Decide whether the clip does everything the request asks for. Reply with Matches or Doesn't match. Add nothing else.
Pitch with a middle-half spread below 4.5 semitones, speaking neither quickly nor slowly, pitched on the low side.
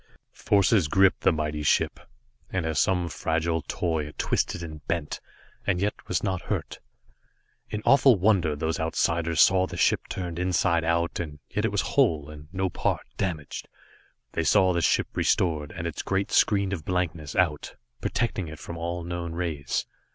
Matches